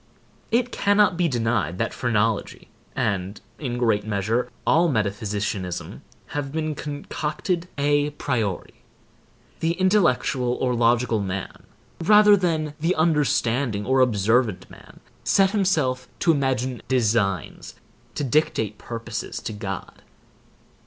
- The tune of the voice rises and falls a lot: Yes, wide, 6.2 semitones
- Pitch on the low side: Yes, low, 125 Hz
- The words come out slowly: Yes, slow, 110 wpm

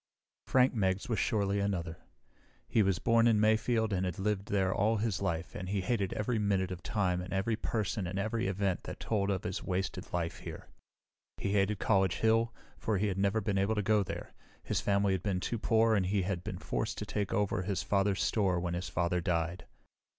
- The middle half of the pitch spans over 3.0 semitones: No, narrow, 2.6 semitones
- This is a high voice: No, low, 100 Hz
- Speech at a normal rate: No, fast, 210 wpm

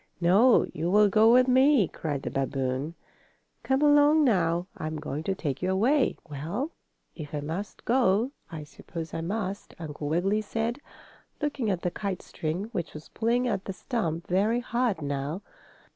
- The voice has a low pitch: No, high, 190 Hz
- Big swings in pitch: Yes, wide, 6.9 semitones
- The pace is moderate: Yes, average, 165 wpm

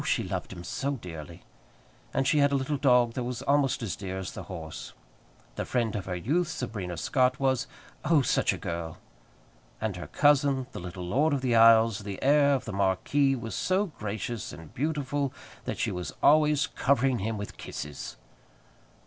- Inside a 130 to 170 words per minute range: No, average, 185 wpm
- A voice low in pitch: Yes, low, 125 Hz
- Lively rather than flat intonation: Yes, wide, 6.5 semitones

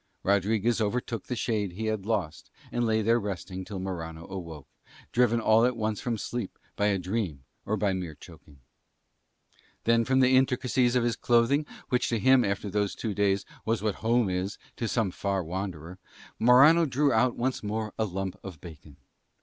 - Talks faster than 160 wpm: Yes, average, 180 wpm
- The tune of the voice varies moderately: Yes, average, 3.9 semitones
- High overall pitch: No, low, 110 Hz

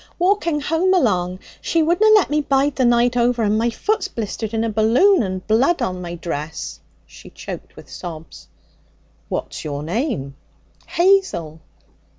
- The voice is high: Yes, high, 235 Hz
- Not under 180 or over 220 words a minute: No, average, 155 wpm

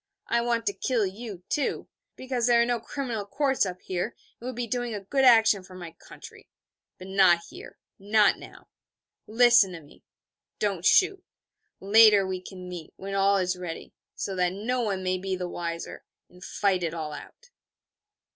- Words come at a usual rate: Yes, average, 185 wpm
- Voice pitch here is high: Yes, high, 200 Hz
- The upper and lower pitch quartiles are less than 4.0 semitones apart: No, average, 4.4 semitones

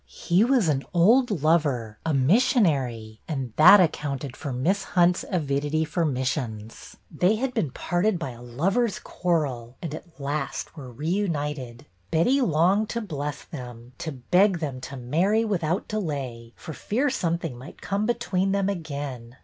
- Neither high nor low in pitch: Yes, medium, 155 Hz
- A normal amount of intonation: No, wide, 6.2 semitones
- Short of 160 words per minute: Yes, average, 150 wpm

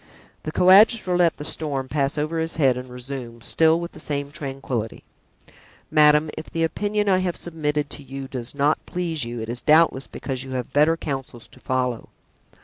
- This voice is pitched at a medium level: Yes, medium, 145 Hz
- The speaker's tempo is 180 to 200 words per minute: Yes, average, 185 wpm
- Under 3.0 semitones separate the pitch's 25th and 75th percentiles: No, average, 3.8 semitones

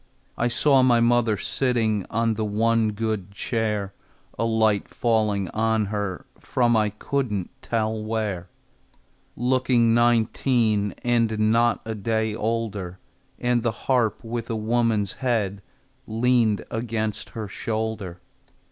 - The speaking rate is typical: No, slow, 120 wpm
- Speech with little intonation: Yes, narrow, 1.8 semitones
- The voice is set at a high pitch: No, low, 110 Hz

